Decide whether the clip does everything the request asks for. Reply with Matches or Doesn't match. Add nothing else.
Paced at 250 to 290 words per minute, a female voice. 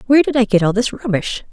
Matches